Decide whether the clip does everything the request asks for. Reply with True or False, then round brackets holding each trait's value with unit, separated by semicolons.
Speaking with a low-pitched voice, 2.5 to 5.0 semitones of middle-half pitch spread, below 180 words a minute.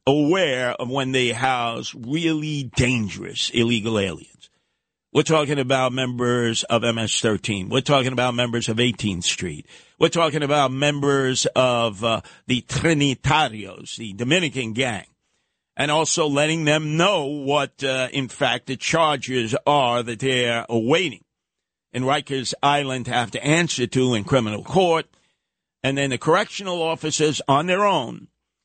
True (130 Hz; 3.6 semitones; 140 wpm)